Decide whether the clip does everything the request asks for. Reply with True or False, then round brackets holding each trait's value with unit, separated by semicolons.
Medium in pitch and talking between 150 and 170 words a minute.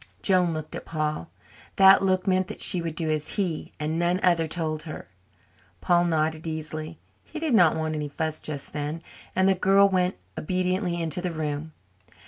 False (165 Hz; 180 wpm)